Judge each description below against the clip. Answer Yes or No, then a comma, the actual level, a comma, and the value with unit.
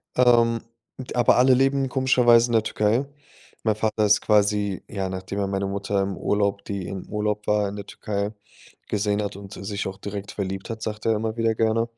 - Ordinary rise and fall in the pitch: No, narrow, 2.3 semitones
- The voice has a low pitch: Yes, low, 105 Hz